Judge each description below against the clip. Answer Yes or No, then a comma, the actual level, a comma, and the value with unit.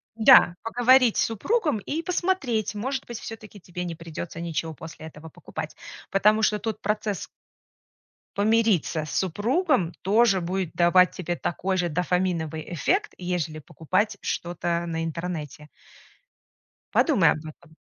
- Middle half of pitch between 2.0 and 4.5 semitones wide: No, average, 5.1 semitones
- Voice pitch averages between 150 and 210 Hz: Yes, medium, 185 Hz